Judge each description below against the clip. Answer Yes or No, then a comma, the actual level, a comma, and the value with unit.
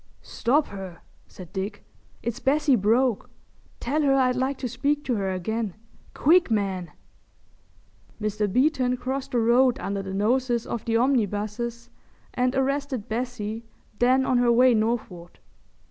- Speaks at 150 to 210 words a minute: No, average, 140 wpm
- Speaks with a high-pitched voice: Yes, high, 240 Hz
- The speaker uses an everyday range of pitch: Yes, average, 3.8 semitones